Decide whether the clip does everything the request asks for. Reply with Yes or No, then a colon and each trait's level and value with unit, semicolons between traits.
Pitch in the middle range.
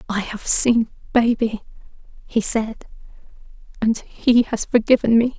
No: high, 225 Hz